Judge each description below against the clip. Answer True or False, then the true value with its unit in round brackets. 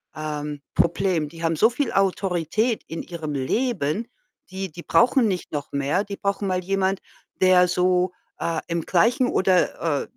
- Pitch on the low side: False (180 Hz)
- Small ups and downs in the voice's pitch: False (3.3 semitones)